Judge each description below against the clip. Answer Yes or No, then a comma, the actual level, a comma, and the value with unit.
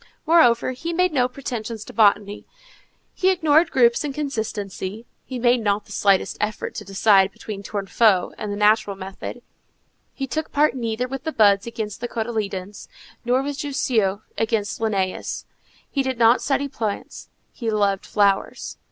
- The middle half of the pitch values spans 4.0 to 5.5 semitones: Yes, average, 4.3 semitones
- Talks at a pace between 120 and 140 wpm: No, average, 155 wpm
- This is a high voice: Yes, high, 225 Hz